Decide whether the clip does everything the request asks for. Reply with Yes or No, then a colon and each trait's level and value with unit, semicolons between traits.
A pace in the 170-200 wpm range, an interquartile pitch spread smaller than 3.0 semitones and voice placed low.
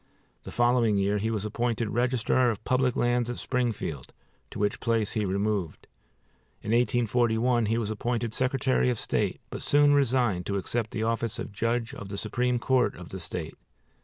Yes: average, 175 wpm; narrow, 2.5 semitones; low, 115 Hz